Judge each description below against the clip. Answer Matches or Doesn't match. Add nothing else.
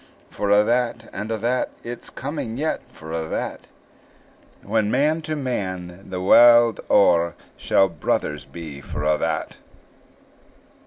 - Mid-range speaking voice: Doesn't match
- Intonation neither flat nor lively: Doesn't match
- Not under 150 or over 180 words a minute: Doesn't match